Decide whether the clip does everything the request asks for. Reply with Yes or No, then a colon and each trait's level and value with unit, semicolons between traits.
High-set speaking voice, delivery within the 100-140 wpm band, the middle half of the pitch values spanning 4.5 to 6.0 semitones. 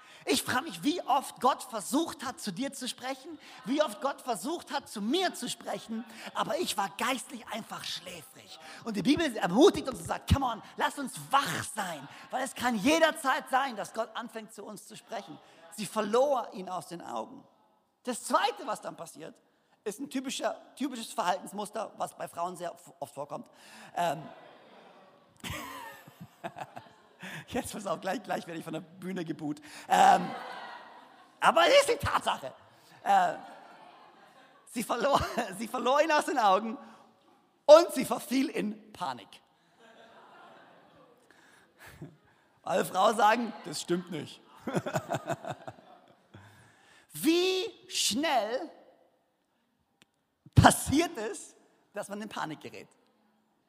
Yes: high, 245 Hz; average, 135 wpm; wide, 5.5 semitones